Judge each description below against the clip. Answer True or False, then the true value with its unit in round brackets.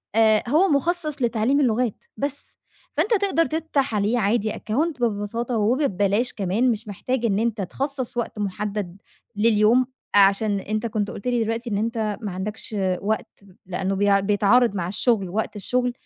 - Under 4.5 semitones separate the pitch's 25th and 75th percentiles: True (3.5 semitones)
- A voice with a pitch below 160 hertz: False (220 Hz)